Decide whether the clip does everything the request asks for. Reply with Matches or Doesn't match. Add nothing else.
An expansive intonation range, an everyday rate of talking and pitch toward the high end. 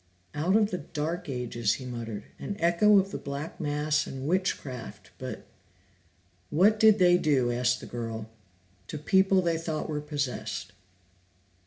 Doesn't match